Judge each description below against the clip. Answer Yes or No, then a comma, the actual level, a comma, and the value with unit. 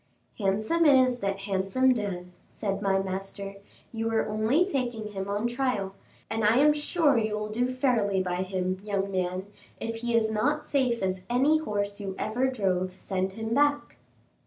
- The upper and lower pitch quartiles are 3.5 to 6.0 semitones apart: Yes, average, 4.5 semitones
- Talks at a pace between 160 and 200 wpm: Yes, average, 170 wpm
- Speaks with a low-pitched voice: No, high, 215 Hz